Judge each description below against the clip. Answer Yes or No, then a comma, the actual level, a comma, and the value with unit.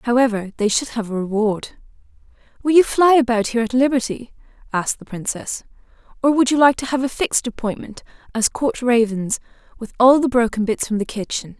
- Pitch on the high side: Yes, high, 240 Hz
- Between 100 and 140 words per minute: No, average, 185 wpm